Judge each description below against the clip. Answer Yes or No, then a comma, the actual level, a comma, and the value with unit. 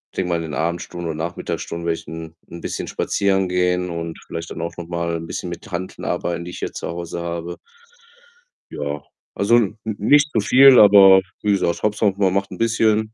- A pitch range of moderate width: Yes, average, 3.1 semitones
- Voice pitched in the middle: No, very low, 90 Hz